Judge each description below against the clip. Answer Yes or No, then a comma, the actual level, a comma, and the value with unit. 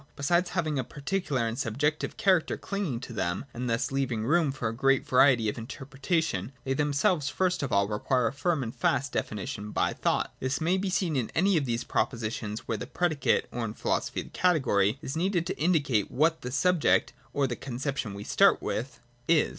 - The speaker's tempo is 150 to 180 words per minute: No, average, 200 wpm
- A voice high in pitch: No, low, 135 Hz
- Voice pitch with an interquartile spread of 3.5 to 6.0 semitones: Yes, wide, 5.6 semitones